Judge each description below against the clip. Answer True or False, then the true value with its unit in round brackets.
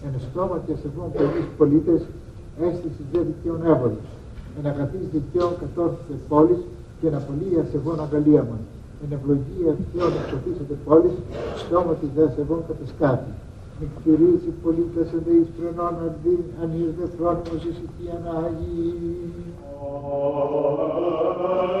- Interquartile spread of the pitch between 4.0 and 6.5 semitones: False (2.8 semitones)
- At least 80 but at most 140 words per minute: True (125 wpm)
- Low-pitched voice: False (160 Hz)